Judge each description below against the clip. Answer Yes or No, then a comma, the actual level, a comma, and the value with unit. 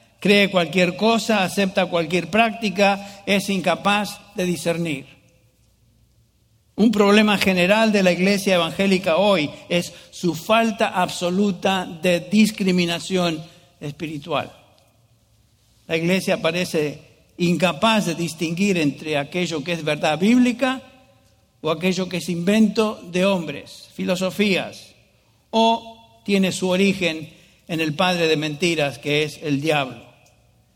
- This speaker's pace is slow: Yes, slow, 115 wpm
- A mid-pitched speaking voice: Yes, medium, 180 Hz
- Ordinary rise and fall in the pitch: Yes, average, 4.6 semitones